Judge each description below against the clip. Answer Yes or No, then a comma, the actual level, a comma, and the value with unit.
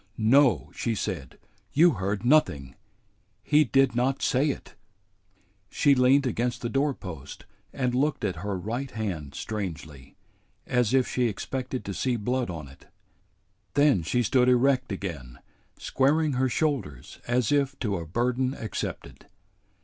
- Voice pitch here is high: No, low, 120 Hz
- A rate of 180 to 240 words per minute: No, average, 140 wpm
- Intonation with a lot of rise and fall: Yes, wide, 5.8 semitones